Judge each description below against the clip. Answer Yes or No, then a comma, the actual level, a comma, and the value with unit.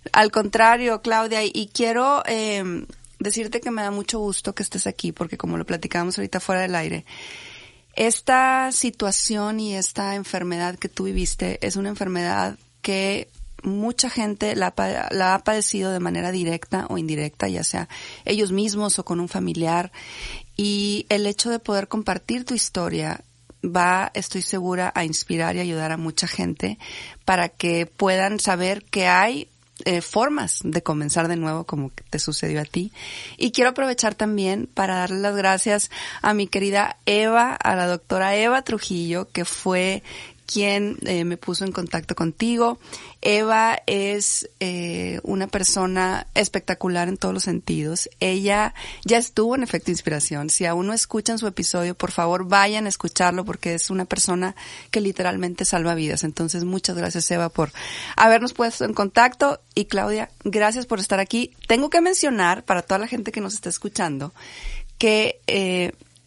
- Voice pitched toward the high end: Yes, high, 195 Hz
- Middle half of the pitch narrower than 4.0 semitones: Yes, average, 3.5 semitones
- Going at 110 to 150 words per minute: No, average, 160 wpm